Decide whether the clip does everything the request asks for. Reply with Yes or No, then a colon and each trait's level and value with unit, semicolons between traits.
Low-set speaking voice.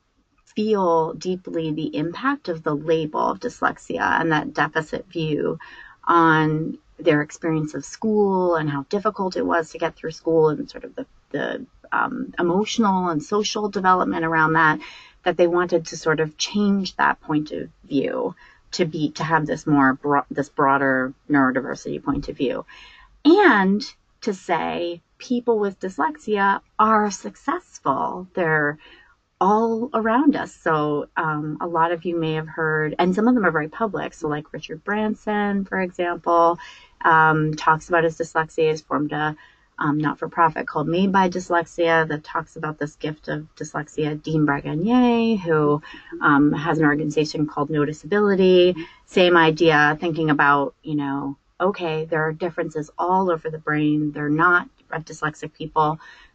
No: medium, 160 Hz